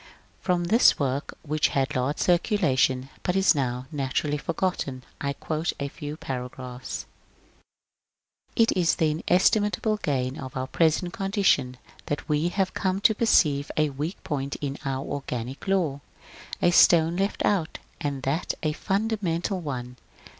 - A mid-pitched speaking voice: Yes, medium, 150 Hz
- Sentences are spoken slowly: No, average, 145 wpm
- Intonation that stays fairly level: No, average, 5.0 semitones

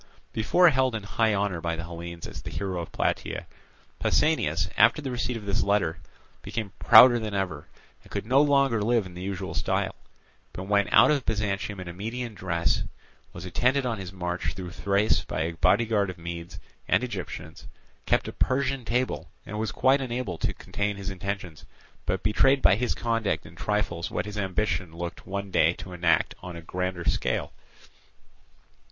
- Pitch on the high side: No, low, 100 Hz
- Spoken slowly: No, average, 180 wpm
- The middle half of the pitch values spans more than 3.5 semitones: Yes, average, 4.6 semitones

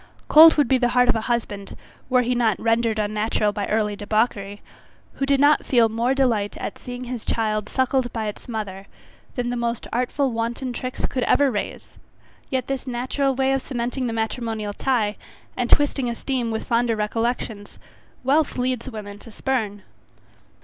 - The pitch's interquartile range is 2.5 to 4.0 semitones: Yes, average, 3.0 semitones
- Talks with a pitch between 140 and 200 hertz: No, high, 235 Hz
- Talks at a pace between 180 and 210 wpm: No, average, 170 wpm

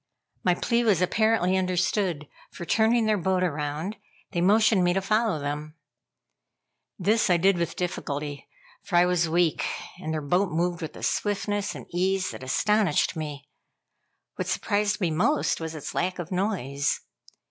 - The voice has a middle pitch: Yes, medium, 180 Hz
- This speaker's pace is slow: No, average, 160 wpm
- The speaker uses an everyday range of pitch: Yes, average, 4.2 semitones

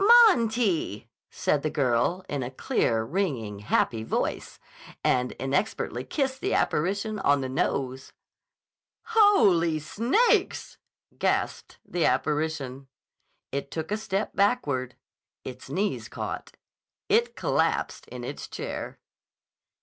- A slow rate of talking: Yes, slow, 110 wpm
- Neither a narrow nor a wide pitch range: No, wide, 8.6 semitones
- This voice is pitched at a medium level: Yes, medium, 155 Hz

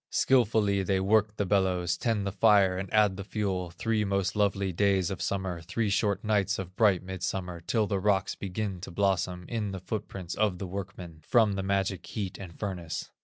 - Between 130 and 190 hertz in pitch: No, very low, 95 Hz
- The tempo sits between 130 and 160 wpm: No, average, 195 wpm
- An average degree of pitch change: No, narrow, 2.0 semitones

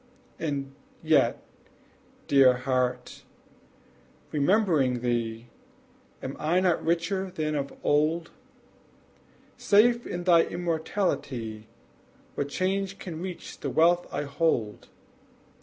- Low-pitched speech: No, medium, 155 Hz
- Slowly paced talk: Yes, slow, 95 wpm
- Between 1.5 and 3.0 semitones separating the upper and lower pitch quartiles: No, average, 5.3 semitones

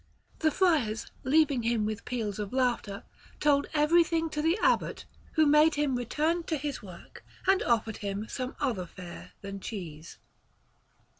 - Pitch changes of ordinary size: No, wide, 6.6 semitones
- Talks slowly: No, average, 150 wpm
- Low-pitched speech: No, very high, 255 Hz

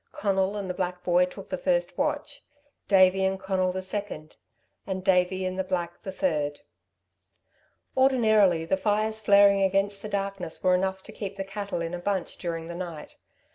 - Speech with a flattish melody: Yes, narrow, 1.8 semitones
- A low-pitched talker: No, high, 190 Hz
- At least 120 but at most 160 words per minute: No, average, 175 wpm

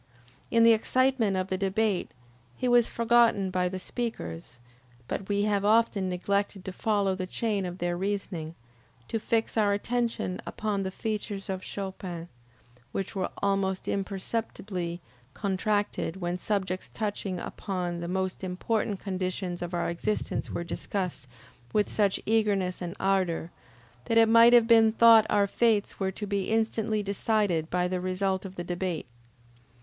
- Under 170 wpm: Yes, average, 150 wpm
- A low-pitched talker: No, high, 195 Hz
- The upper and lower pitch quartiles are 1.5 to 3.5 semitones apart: Yes, average, 2.9 semitones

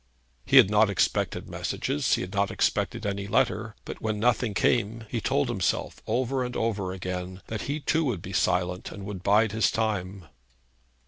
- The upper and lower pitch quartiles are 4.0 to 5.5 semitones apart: No, average, 3.1 semitones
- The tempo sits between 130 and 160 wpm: No, average, 180 wpm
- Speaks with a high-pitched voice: No, low, 105 Hz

